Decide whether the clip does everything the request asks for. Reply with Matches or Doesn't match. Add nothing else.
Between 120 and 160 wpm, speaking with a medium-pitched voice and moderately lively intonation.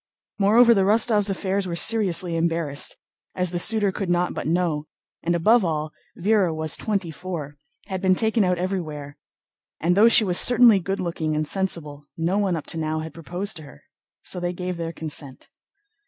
Doesn't match